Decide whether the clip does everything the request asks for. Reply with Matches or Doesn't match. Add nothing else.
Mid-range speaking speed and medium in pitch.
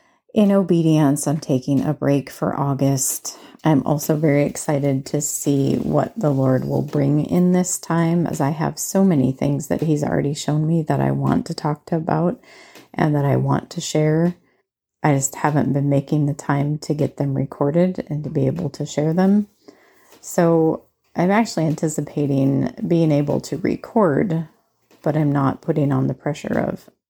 Matches